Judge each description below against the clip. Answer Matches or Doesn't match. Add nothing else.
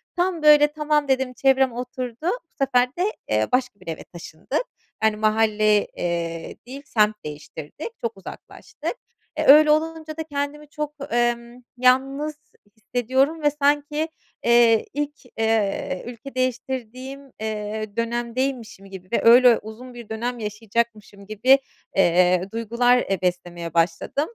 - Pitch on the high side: Matches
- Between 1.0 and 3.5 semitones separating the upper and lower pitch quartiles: Doesn't match